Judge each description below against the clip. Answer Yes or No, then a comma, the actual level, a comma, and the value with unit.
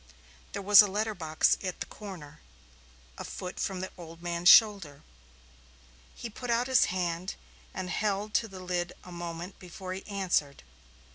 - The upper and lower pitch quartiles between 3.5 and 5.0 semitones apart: No, average, 2.9 semitones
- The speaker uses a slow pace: No, average, 155 wpm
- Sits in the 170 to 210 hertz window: Yes, medium, 185 Hz